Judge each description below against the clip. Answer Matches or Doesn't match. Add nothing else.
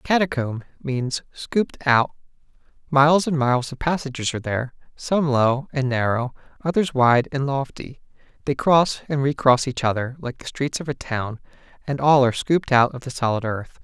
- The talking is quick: Doesn't match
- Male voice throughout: Matches